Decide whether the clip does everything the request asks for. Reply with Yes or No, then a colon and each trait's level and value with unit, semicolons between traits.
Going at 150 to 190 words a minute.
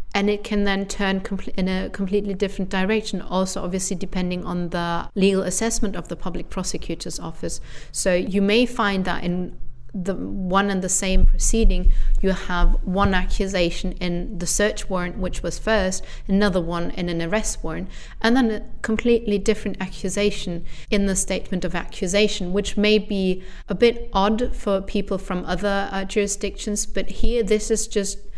Yes: average, 165 wpm